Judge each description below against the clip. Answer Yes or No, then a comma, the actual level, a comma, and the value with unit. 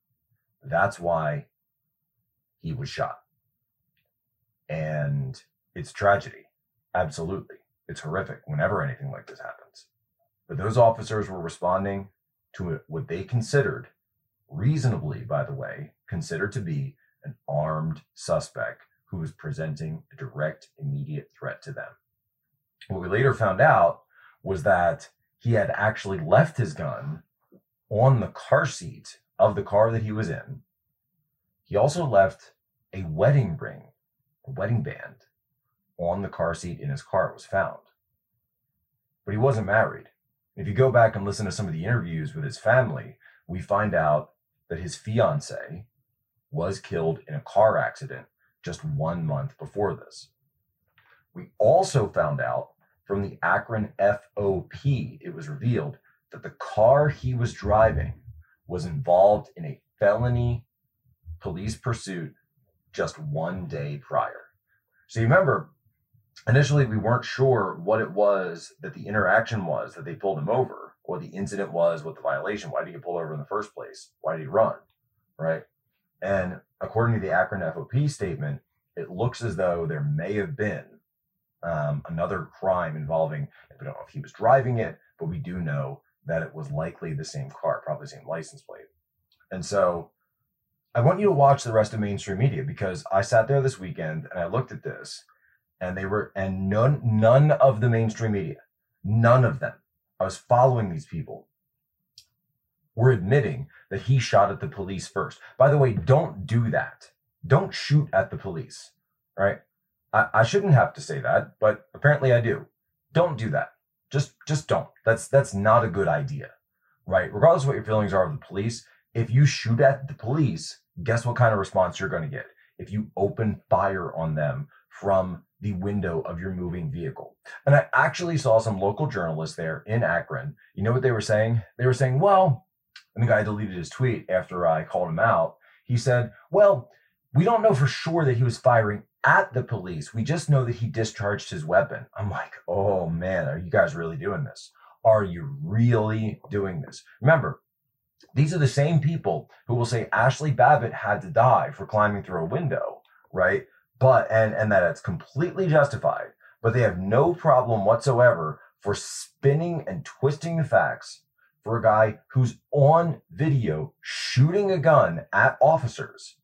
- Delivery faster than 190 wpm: No, average, 170 wpm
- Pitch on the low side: Yes, low, 120 Hz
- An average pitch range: No, wide, 5.7 semitones